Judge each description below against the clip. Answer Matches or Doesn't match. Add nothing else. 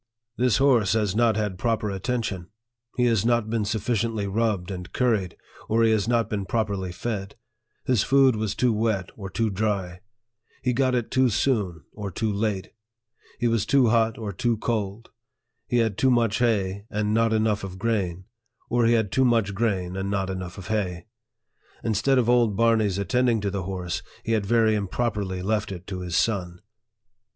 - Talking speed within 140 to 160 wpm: Doesn't match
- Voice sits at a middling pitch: Doesn't match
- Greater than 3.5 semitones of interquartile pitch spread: Doesn't match